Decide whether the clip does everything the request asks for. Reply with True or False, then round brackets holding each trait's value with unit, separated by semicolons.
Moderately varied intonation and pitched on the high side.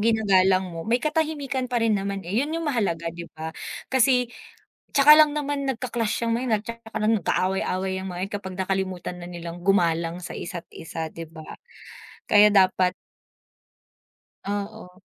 False (5.7 semitones; 200 Hz)